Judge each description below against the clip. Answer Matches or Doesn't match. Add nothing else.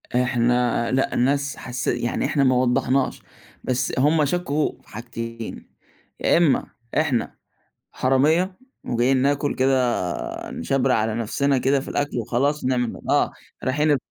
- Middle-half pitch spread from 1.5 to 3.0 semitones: Matches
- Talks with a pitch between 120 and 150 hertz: Matches